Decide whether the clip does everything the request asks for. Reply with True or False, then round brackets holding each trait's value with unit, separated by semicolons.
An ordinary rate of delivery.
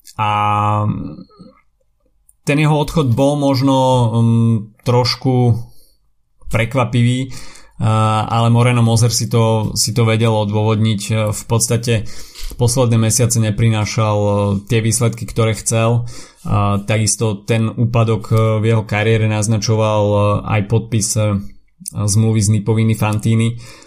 False (100 wpm)